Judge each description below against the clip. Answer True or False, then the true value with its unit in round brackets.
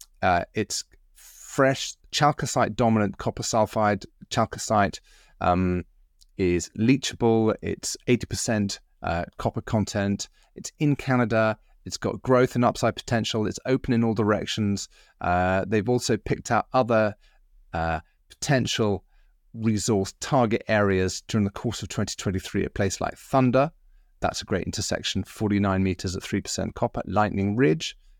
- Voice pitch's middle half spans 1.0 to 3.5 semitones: False (3.9 semitones)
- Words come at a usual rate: False (130 wpm)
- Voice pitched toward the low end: True (110 Hz)